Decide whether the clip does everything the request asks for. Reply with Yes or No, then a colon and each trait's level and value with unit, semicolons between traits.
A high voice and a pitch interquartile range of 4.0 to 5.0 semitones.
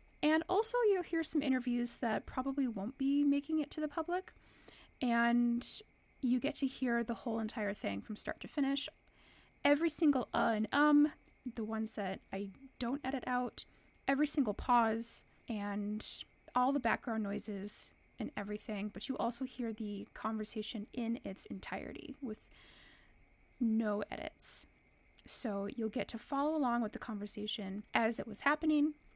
Yes: high, 240 Hz; average, 4.5 semitones